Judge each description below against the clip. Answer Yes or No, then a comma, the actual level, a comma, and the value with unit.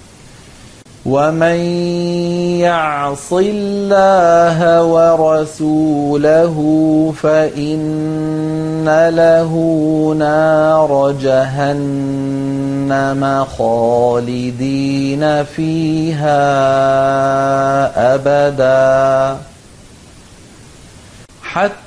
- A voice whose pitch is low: No, medium, 155 Hz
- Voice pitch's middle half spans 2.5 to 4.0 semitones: Yes, average, 2.8 semitones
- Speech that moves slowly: Yes, slow, 30 wpm